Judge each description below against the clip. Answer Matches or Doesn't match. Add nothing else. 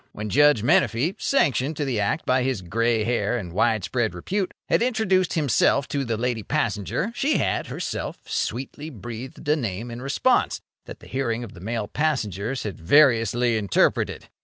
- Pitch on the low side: Matches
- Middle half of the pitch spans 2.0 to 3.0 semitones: Doesn't match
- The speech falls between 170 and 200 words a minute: Doesn't match